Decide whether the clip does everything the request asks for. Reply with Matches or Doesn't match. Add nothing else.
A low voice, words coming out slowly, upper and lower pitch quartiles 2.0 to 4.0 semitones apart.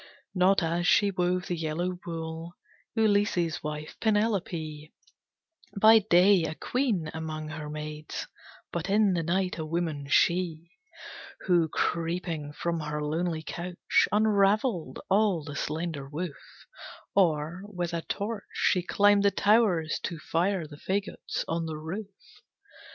Doesn't match